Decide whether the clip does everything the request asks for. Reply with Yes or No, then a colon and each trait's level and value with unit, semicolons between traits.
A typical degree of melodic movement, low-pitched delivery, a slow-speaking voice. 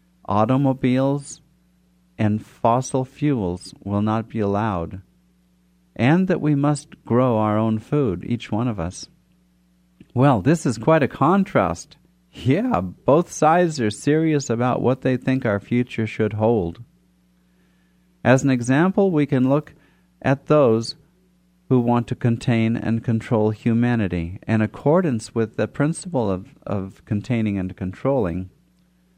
No: wide, 6.0 semitones; low, 120 Hz; slow, 130 wpm